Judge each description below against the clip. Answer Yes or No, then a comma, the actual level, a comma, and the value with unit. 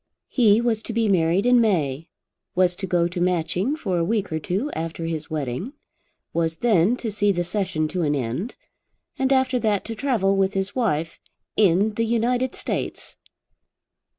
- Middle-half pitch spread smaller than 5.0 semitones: No, wide, 5.4 semitones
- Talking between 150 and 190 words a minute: Yes, average, 175 wpm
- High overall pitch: Yes, high, 195 Hz